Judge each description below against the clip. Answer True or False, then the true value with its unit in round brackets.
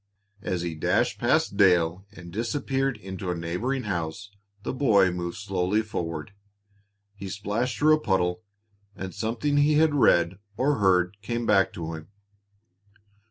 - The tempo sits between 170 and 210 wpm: False (145 wpm)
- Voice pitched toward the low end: True (100 Hz)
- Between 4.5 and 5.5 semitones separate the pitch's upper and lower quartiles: True (5.0 semitones)